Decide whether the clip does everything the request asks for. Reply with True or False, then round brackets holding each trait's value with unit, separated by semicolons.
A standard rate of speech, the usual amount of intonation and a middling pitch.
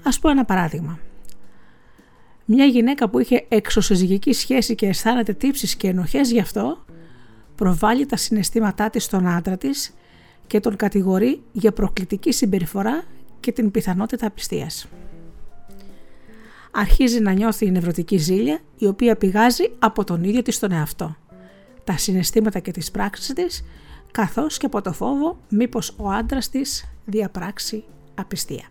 False (140 wpm; 4.6 semitones; 210 Hz)